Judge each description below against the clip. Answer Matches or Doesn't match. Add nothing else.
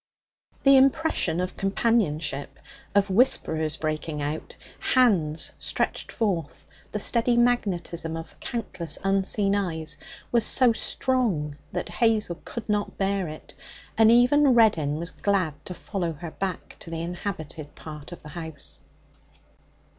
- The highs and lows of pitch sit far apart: Matches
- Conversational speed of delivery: Doesn't match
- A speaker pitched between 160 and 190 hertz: Matches